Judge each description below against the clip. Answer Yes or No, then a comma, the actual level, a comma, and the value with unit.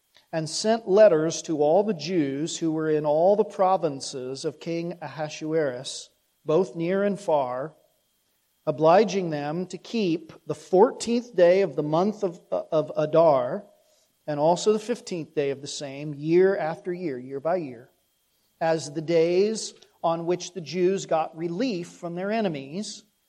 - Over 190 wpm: No, average, 150 wpm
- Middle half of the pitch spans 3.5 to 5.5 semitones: Yes, average, 3.9 semitones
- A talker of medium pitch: Yes, medium, 170 Hz